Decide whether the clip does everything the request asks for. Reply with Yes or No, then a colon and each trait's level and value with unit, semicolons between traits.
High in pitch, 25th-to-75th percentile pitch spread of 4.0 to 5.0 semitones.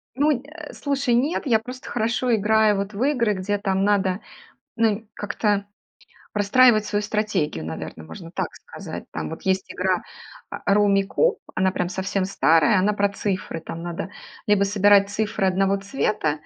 No: high, 205 Hz; narrow, 2.6 semitones